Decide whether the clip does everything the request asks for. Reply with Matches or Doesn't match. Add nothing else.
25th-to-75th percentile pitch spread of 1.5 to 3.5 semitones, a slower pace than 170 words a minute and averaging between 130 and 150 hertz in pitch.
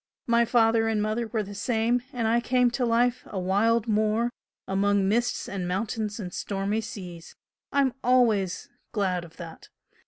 Doesn't match